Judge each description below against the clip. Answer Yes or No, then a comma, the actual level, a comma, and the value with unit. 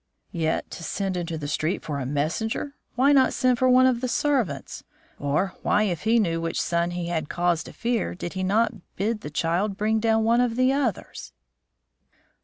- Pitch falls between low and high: No, high, 200 Hz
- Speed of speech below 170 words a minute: No, average, 200 wpm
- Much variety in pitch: Yes, wide, 5.9 semitones